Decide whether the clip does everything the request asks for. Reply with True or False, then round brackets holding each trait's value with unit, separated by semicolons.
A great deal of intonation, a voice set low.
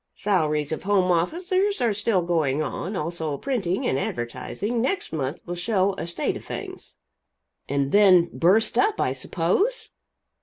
False (5.8 semitones; 180 Hz)